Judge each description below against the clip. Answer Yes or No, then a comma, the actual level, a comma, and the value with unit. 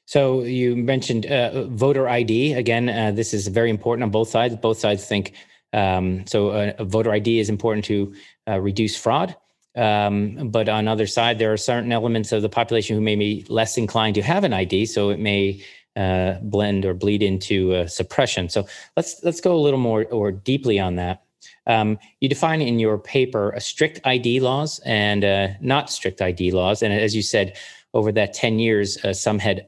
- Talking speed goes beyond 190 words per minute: Yes, average, 200 wpm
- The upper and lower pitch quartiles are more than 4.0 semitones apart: No, average, 2.7 semitones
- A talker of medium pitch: No, low, 110 Hz